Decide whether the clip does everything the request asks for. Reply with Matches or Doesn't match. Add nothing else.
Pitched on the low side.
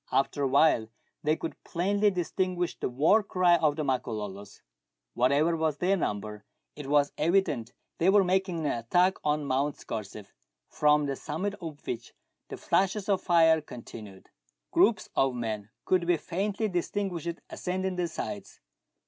Doesn't match